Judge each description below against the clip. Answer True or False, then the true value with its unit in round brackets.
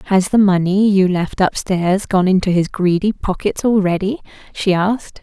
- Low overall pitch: False (190 Hz)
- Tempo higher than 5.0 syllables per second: False (4.7 syllables/s)